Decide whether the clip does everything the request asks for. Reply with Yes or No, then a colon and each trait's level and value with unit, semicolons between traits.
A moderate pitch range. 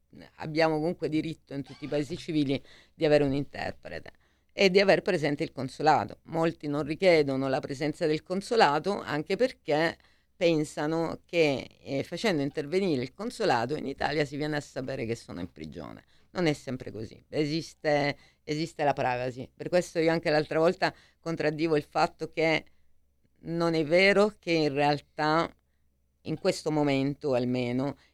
Yes: average, 3.1 semitones